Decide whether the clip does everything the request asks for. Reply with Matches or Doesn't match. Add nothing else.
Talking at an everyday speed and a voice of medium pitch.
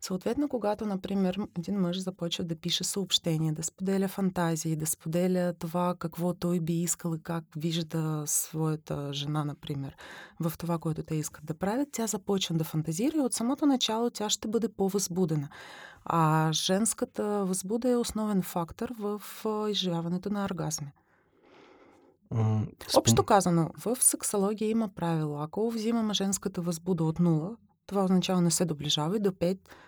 Matches